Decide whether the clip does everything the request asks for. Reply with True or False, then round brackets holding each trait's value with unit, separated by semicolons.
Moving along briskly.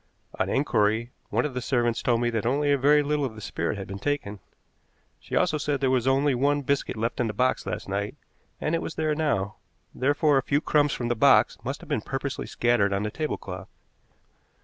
True (215 wpm)